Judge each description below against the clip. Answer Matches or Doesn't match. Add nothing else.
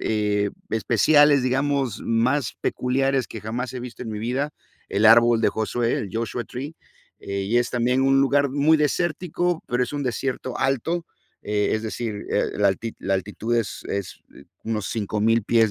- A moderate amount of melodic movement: Matches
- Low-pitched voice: Matches